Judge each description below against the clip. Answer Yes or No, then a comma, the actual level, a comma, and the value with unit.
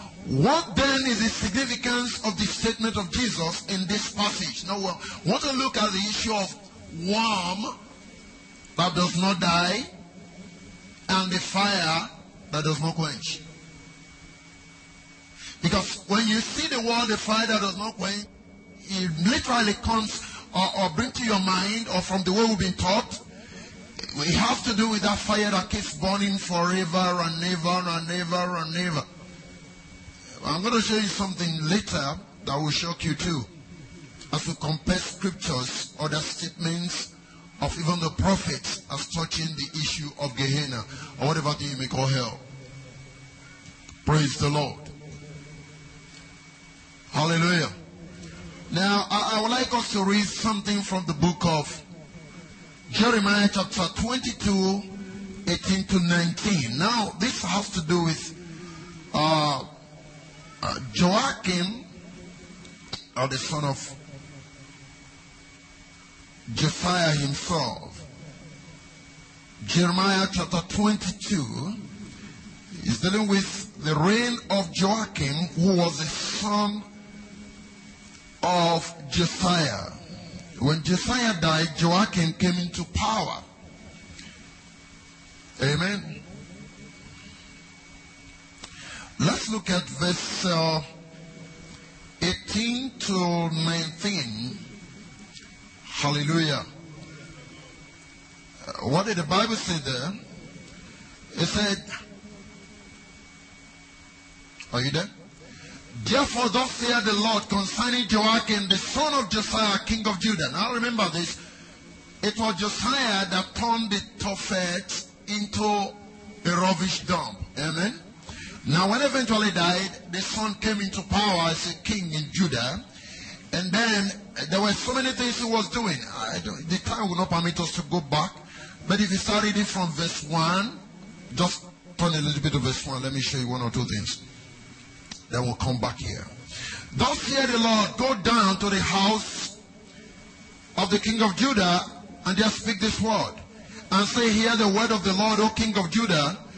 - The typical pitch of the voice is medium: Yes, medium, 180 Hz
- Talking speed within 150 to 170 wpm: No, slow, 135 wpm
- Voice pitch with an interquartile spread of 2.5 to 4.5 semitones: No, average, 5.1 semitones